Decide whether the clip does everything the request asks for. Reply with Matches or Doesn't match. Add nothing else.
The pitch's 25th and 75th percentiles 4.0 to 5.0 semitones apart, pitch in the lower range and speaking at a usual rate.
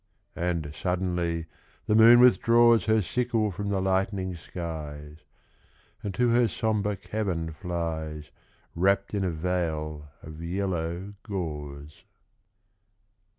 Doesn't match